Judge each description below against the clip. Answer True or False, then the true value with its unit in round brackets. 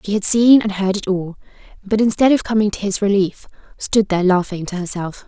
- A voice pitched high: True (200 Hz)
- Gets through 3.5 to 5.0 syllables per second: False (5.7 syllables/s)